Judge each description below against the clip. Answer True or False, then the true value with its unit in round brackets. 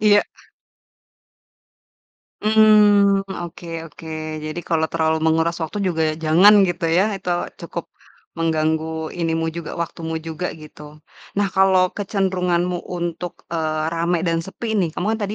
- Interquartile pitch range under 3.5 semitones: True (3.0 semitones)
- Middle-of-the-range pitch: True (170 Hz)